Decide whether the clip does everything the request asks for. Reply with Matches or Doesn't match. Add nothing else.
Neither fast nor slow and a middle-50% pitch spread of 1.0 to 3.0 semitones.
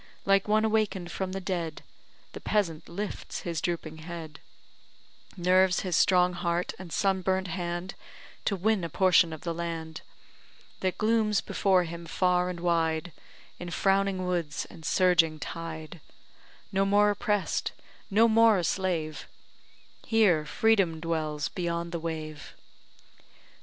Doesn't match